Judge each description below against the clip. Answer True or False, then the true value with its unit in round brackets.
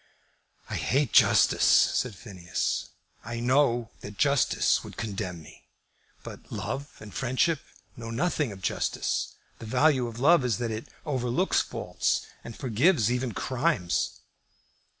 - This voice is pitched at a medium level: False (120 Hz)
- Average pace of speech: False (130 wpm)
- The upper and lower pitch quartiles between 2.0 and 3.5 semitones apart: False (4.2 semitones)